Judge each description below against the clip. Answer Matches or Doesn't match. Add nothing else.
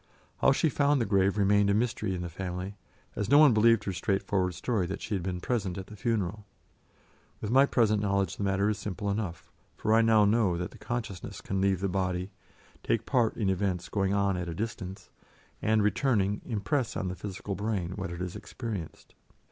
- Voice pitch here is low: Matches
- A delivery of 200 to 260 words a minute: Matches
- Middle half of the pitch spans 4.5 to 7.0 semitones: Doesn't match